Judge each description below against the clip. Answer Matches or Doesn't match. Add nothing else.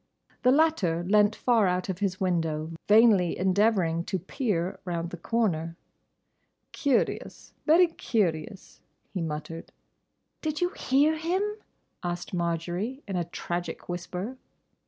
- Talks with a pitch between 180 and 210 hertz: Matches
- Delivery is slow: Matches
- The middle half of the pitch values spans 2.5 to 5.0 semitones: Doesn't match